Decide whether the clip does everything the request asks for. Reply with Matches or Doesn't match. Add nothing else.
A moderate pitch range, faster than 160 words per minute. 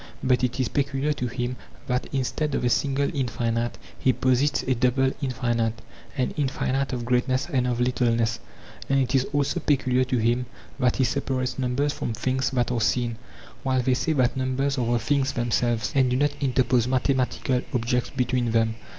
Doesn't match